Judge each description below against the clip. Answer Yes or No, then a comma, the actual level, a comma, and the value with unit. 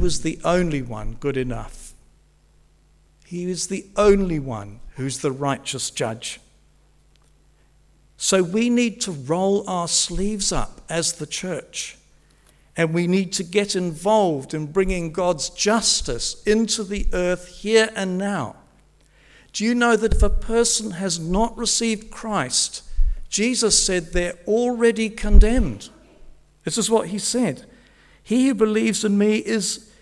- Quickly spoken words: No, average, 140 wpm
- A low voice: No, high, 190 Hz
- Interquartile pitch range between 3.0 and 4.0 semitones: No, wide, 5.6 semitones